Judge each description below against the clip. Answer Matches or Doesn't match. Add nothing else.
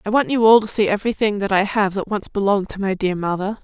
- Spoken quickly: Matches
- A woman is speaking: Matches